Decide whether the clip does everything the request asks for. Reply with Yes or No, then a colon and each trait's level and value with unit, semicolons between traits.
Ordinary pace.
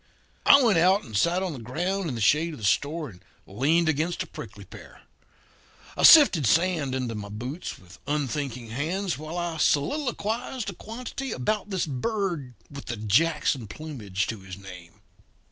Yes: average, 170 wpm